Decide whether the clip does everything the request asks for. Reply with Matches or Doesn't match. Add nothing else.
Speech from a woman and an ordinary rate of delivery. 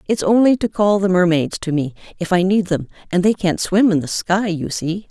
Doesn't match